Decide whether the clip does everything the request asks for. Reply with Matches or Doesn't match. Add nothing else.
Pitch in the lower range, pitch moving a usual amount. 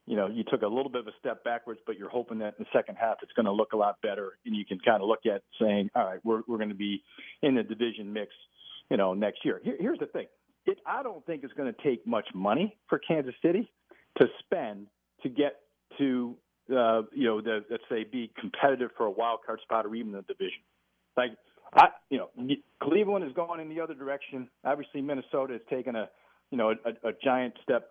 Matches